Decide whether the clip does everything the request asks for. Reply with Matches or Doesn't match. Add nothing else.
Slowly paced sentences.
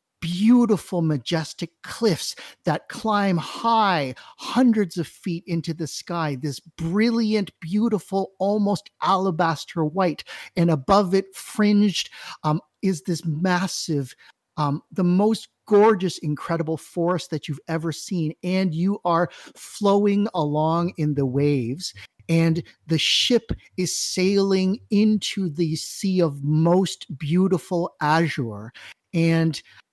Matches